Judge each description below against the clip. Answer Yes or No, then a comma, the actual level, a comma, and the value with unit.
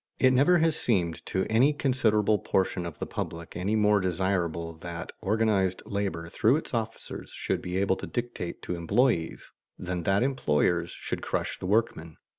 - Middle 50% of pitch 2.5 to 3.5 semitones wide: No, average, 4.6 semitones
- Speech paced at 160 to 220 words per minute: Yes, average, 165 wpm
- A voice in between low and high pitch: No, low, 100 Hz